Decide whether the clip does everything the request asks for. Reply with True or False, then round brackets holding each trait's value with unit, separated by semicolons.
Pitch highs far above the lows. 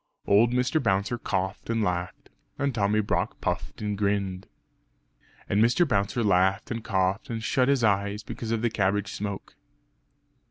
False (3.0 semitones)